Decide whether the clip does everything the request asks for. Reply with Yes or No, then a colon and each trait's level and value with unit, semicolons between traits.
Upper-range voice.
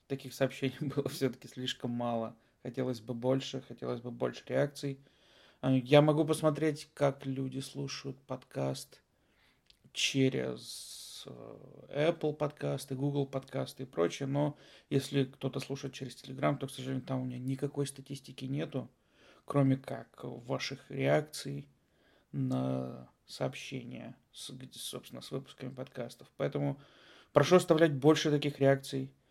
No: low, 135 Hz